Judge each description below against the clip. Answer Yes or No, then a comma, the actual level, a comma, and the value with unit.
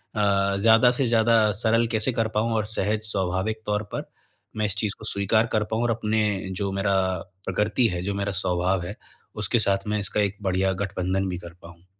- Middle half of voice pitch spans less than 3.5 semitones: Yes, narrow, 2.4 semitones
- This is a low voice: Yes, low, 105 Hz